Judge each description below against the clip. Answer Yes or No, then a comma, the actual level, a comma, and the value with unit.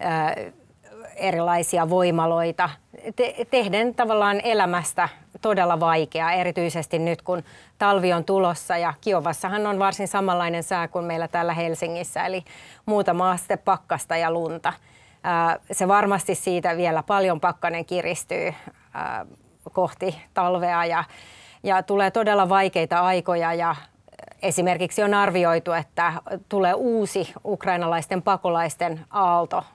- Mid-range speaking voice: Yes, medium, 180 Hz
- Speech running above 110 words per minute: No, average, 105 wpm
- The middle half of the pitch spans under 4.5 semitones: Yes, narrow, 2.5 semitones